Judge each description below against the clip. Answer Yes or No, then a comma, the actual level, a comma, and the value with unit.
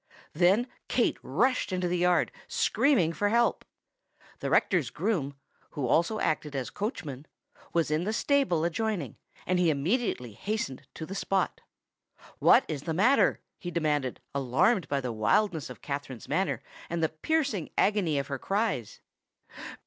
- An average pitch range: No, wide, 6.7 semitones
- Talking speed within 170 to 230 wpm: No, average, 150 wpm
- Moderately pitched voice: Yes, medium, 170 Hz